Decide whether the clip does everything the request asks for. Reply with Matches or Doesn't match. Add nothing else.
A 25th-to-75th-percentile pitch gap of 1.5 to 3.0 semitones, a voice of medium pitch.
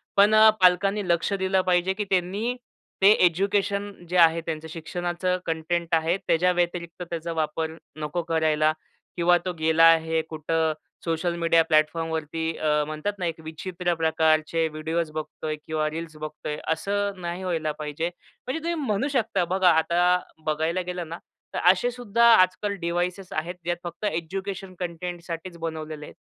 Matches